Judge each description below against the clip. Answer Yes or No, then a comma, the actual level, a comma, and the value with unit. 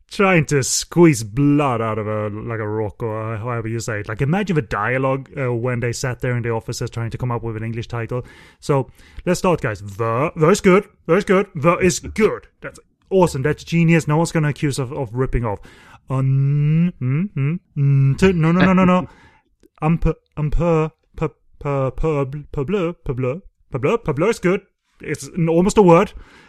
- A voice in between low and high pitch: Yes, medium, 145 Hz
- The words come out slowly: No, average, 190 wpm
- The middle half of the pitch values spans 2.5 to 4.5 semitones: No, wide, 5.5 semitones